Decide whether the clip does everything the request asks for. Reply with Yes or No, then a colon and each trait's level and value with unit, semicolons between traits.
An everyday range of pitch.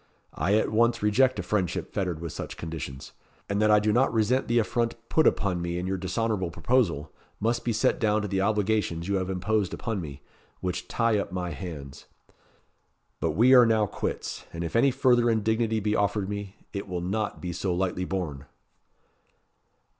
Yes: average, 3.8 semitones